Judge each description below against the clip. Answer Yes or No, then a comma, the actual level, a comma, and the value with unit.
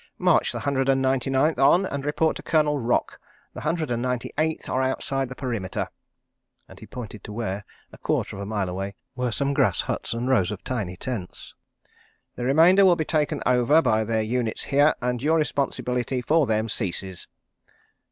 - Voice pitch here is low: Yes, low, 130 Hz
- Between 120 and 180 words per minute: No, average, 190 wpm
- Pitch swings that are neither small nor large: Yes, average, 4.6 semitones